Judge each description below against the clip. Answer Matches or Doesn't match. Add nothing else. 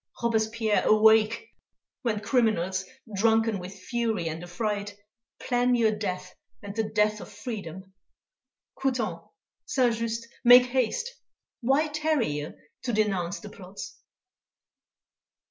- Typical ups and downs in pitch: Matches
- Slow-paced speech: Matches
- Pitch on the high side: Matches